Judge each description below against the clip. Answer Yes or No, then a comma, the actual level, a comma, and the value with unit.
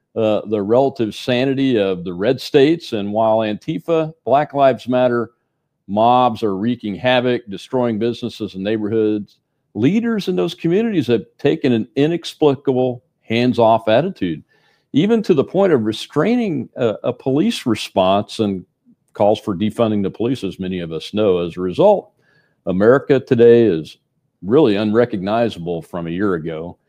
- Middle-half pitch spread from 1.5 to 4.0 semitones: No, average, 4.7 semitones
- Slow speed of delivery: No, average, 145 wpm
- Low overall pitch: Yes, low, 115 Hz